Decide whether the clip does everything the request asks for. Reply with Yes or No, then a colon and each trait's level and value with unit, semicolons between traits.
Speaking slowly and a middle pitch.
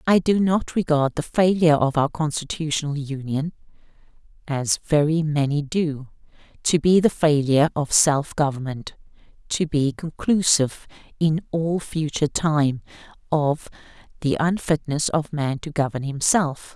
Yes: slow, 125 wpm; medium, 155 Hz